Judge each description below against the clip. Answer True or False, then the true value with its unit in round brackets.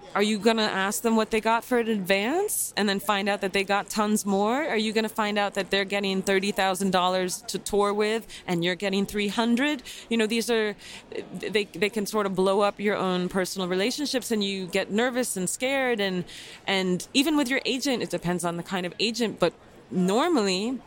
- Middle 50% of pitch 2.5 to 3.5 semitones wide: True (2.8 semitones)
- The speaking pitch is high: True (205 Hz)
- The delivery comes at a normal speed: False (215 wpm)